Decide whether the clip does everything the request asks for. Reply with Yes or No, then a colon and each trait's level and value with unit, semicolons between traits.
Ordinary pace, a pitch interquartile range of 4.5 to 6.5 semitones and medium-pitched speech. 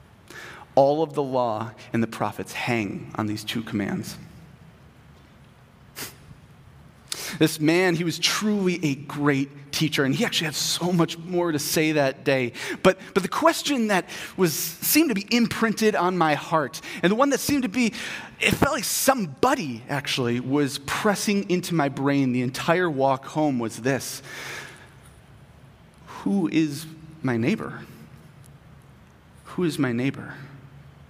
Yes: average, 145 wpm; average, 5.0 semitones; medium, 155 Hz